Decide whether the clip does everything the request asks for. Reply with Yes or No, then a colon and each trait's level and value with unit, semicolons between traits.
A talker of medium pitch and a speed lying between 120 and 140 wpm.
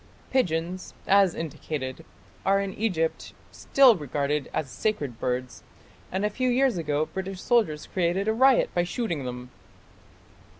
Yes: medium, 175 Hz; slow, 135 wpm